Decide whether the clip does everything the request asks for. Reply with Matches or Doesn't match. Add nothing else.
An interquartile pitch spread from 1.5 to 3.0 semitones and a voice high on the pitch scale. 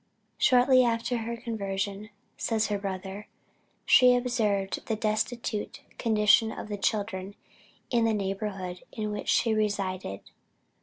Matches